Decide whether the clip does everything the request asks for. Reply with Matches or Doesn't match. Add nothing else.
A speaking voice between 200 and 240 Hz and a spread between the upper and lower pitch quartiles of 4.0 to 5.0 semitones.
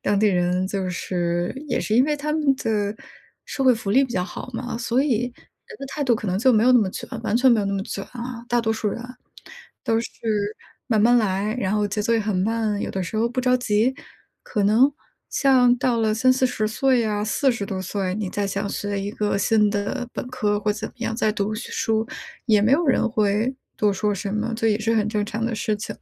Doesn't match